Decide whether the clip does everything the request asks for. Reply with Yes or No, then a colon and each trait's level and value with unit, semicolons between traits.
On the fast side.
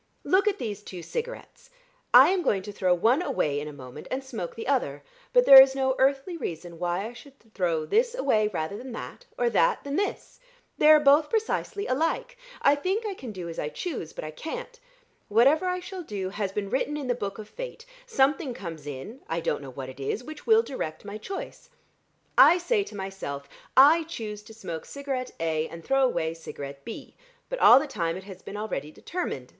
Yes: fast, 210 wpm